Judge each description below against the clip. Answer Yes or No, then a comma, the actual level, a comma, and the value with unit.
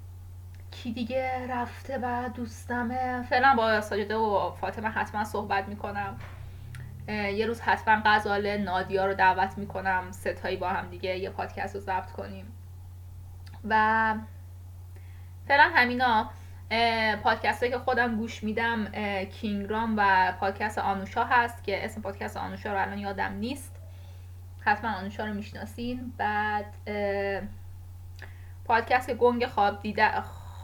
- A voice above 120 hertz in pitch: Yes, high, 190 Hz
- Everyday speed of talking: Yes, average, 120 wpm